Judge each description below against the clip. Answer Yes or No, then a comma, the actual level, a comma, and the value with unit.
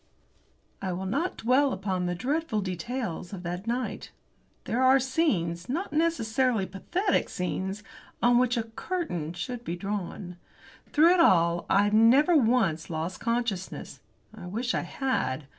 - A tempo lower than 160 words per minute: Yes, average, 140 wpm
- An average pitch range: No, wide, 6.3 semitones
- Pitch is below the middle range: No, high, 220 Hz